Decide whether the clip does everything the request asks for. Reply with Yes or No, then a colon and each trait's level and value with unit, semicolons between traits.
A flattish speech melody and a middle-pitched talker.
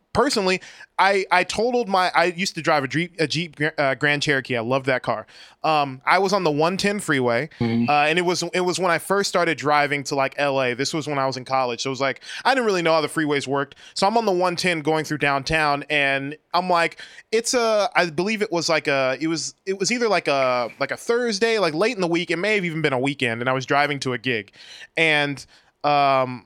No: average, 4.6 semitones; medium, 155 Hz